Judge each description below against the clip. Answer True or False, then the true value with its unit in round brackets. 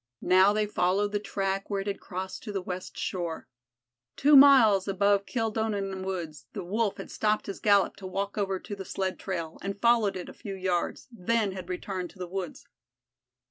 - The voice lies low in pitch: False (195 Hz)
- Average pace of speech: True (190 wpm)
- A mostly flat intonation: True (1.9 semitones)